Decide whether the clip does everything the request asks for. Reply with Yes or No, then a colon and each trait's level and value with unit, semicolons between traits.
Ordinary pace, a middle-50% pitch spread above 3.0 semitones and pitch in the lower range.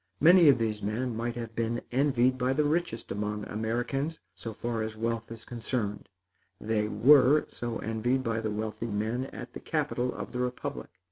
No: average, 180 wpm; average, 2.7 semitones; low, 115 Hz